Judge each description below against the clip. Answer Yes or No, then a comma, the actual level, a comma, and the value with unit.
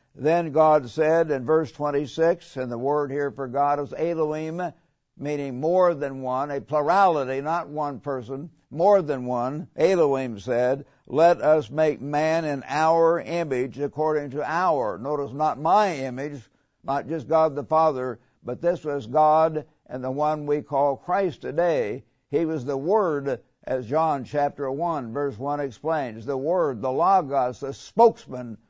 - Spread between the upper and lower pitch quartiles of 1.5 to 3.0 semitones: Yes, average, 2.7 semitones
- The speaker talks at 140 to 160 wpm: Yes, average, 155 wpm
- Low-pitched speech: No, medium, 145 Hz